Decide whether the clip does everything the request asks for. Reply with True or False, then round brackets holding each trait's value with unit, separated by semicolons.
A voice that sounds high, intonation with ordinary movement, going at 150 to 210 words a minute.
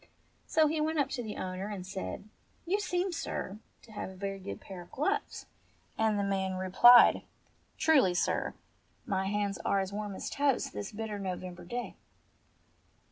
False (205 Hz; 5.7 semitones; 170 wpm)